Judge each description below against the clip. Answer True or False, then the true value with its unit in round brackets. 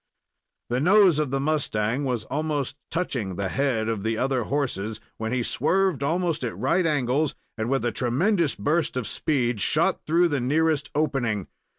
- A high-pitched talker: False (135 Hz)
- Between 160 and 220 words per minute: True (170 wpm)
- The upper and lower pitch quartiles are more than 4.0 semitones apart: True (4.8 semitones)